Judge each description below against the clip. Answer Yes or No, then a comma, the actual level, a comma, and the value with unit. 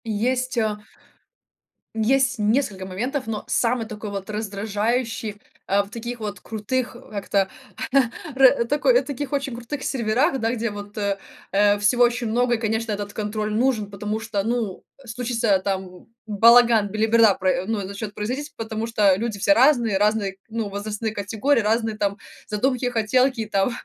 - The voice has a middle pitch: No, high, 220 Hz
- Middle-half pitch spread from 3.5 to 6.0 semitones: No, average, 2.9 semitones